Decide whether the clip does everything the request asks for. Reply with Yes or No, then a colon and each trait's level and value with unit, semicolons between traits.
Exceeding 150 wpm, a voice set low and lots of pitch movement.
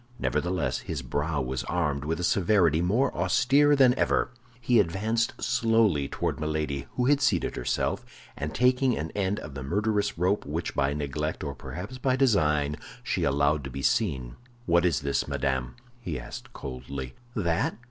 Yes: average, 165 wpm; very low, 85 Hz; wide, 7.4 semitones